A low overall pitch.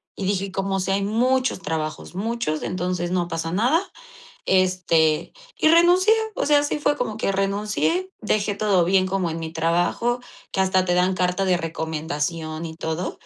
No: medium, 185 Hz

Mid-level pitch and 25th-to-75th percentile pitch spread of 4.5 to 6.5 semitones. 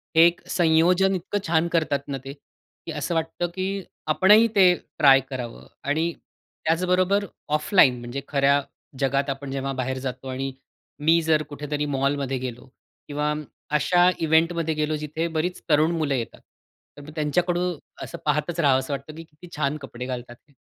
No: medium, 150 Hz; average, 3.7 semitones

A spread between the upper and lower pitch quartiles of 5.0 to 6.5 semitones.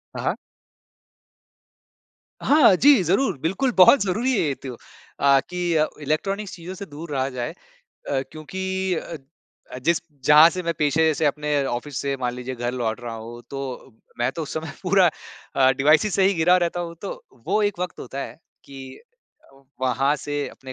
Yes: wide, 5.4 semitones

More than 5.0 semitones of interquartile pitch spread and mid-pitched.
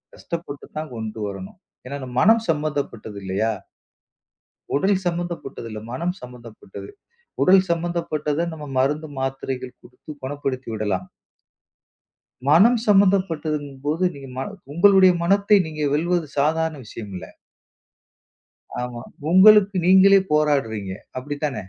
Yes: wide, 5.6 semitones; medium, 150 Hz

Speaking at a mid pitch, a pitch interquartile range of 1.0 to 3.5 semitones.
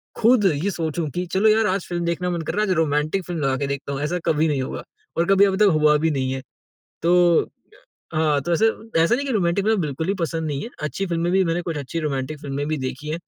No: medium, 165 Hz; average, 3.9 semitones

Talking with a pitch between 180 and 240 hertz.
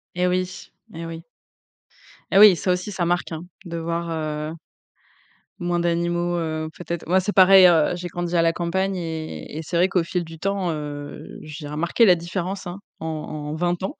No: medium, 170 Hz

